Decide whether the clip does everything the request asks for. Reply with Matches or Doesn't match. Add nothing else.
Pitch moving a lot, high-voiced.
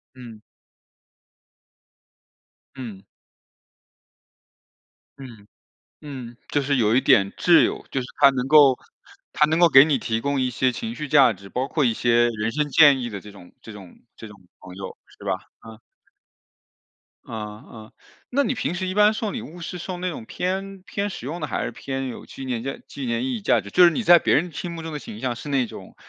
Doesn't match